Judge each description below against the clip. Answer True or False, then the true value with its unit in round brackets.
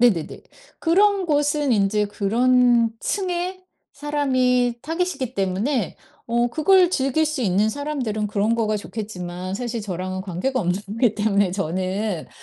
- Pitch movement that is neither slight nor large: False (6.4 semitones)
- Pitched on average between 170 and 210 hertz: False (230 Hz)